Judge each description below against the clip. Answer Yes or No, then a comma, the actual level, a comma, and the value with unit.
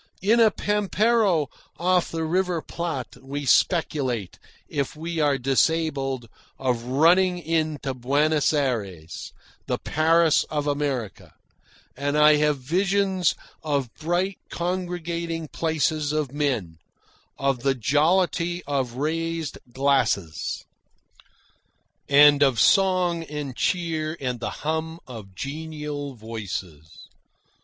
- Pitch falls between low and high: Yes, medium, 150 Hz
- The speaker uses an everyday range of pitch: Yes, average, 3.9 semitones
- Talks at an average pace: No, slow, 110 wpm